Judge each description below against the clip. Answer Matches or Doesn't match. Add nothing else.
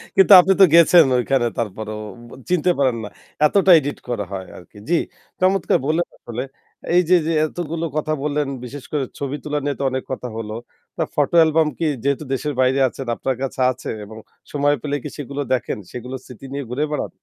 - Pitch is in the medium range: Matches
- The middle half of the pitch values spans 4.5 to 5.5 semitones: Doesn't match